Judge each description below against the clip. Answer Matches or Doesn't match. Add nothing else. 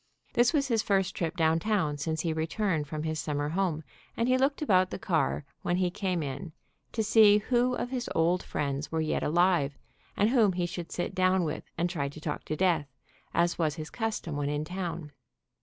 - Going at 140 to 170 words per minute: Doesn't match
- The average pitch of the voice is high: Doesn't match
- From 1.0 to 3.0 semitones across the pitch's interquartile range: Doesn't match